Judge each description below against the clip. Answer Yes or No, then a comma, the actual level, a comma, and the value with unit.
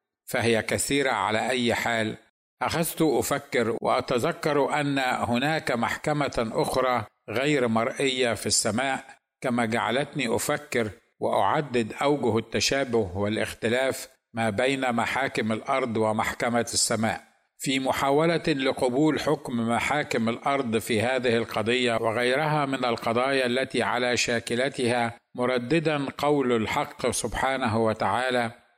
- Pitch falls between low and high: No, low, 125 Hz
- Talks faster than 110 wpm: No, average, 100 wpm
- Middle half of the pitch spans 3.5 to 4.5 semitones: No, average, 3.1 semitones